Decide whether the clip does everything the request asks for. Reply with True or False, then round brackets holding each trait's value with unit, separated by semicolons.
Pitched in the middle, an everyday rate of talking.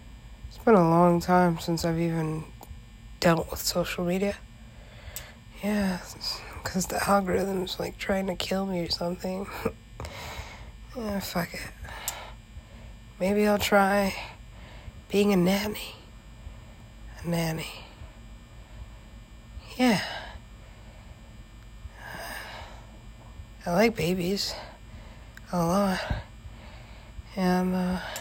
False (175 Hz; 90 wpm)